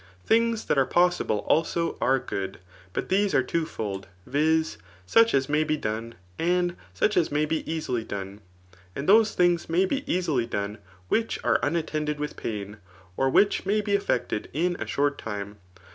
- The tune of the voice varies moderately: No, wide, 7.5 semitones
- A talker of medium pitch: Yes, medium, 155 Hz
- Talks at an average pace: Yes, average, 165 wpm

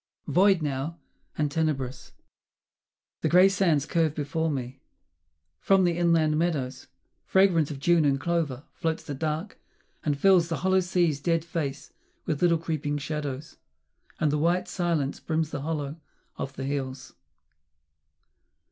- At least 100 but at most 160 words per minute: Yes, average, 140 wpm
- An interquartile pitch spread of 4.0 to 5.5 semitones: No, average, 3.2 semitones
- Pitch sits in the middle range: Yes, medium, 155 Hz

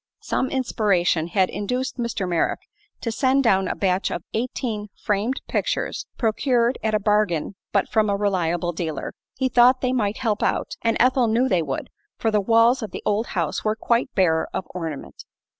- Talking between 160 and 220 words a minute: Yes, average, 180 wpm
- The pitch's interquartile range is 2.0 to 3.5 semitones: No, average, 4.5 semitones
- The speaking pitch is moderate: No, high, 215 Hz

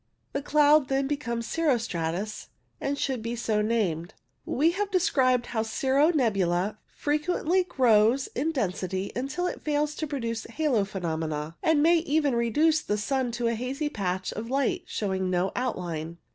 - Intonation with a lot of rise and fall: Yes, wide, 6.5 semitones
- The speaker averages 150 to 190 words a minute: Yes, average, 160 wpm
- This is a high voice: Yes, high, 245 Hz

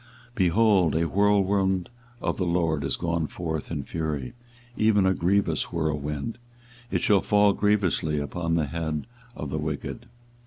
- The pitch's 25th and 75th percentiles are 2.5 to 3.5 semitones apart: No, average, 4.3 semitones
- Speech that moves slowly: No, average, 150 wpm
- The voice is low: Yes, very low, 85 Hz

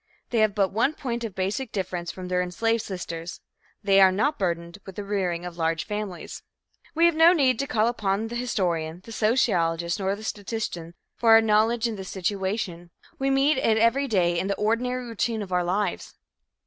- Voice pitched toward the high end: Yes, high, 205 Hz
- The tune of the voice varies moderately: Yes, average, 4.2 semitones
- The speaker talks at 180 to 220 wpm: Yes, average, 195 wpm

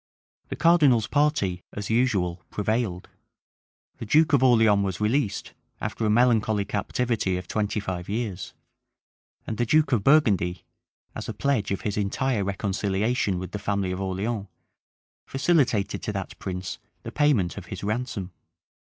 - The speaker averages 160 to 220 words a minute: No, average, 145 wpm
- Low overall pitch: Yes, low, 105 Hz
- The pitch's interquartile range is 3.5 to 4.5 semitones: Yes, average, 4.2 semitones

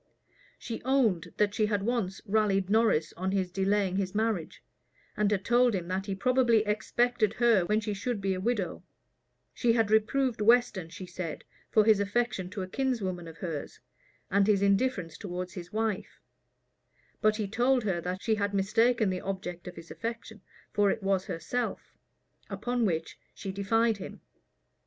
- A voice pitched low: No, high, 205 Hz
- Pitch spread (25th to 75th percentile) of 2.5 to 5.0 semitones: Yes, average, 3.2 semitones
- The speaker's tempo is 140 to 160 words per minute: No, average, 170 wpm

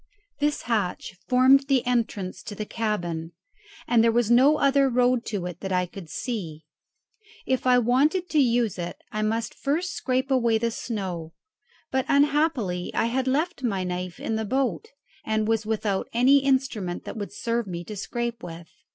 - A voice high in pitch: Yes, high, 230 Hz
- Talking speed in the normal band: Yes, average, 175 wpm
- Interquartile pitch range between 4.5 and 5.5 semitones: Yes, average, 5.2 semitones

